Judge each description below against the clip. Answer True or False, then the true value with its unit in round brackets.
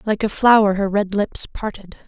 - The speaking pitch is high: True (205 Hz)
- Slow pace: False (200 wpm)